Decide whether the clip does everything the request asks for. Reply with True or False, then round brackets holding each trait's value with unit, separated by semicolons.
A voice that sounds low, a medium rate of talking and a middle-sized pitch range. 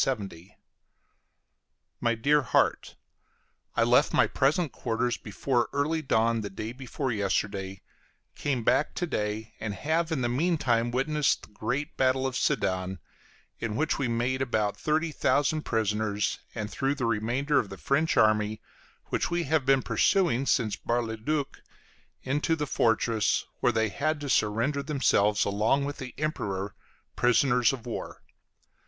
True (125 Hz; 150 wpm; 4.7 semitones)